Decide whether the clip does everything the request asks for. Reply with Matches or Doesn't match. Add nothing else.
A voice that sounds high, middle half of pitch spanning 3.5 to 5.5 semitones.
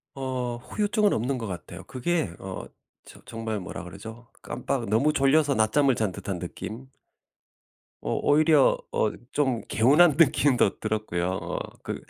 Doesn't match